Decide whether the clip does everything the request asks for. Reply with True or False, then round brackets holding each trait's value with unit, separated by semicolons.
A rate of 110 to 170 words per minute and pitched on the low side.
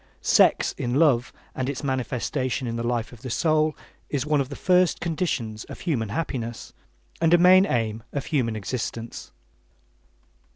True (160 wpm; 130 Hz)